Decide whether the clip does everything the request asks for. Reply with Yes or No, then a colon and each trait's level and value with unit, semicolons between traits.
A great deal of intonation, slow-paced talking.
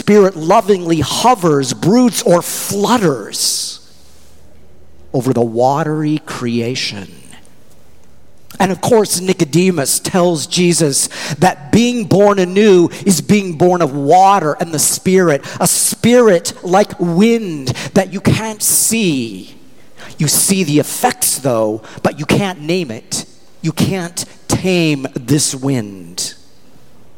Yes: wide, 6.3 semitones; slow, 115 wpm